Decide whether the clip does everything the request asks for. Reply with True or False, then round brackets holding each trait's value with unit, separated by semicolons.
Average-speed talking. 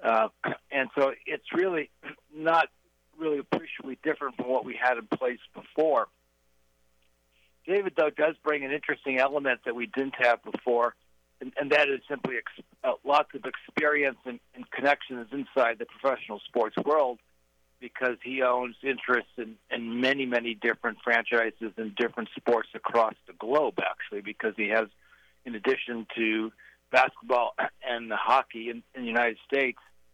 True (155 wpm)